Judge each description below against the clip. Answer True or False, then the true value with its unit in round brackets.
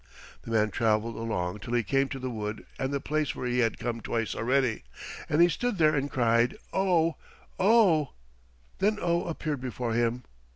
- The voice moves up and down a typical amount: True (5.0 semitones)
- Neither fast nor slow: True (180 wpm)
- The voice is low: True (125 Hz)